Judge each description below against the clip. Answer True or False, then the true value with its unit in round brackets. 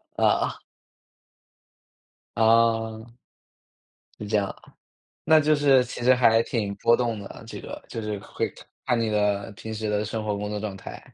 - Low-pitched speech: True (110 Hz)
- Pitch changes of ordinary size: False (2.0 semitones)